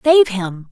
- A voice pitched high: Yes, high, 225 Hz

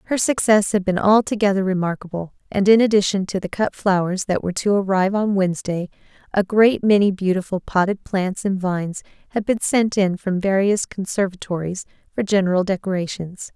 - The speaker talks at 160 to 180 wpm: Yes, average, 165 wpm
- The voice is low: No, high, 195 Hz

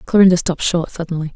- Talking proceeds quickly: No, average, 175 wpm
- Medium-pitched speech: Yes, medium, 170 Hz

